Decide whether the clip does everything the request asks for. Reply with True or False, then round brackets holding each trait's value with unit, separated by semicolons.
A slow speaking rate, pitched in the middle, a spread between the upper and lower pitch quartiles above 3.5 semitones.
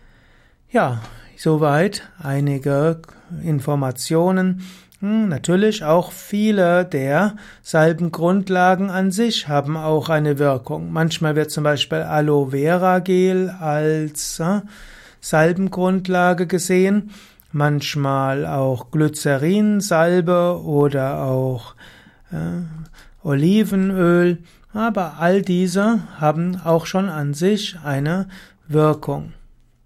True (90 wpm; 165 Hz; 3.9 semitones)